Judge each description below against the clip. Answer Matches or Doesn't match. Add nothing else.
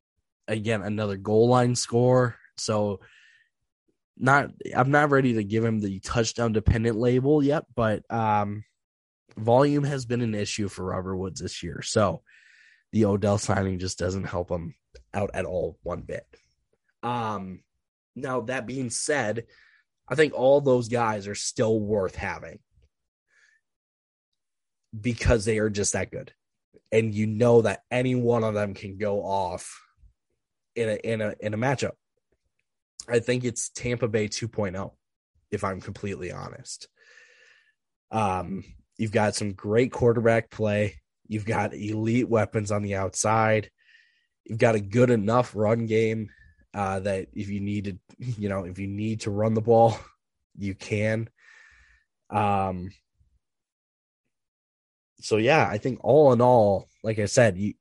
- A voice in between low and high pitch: Doesn't match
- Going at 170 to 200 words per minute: Doesn't match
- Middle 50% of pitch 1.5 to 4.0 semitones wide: Matches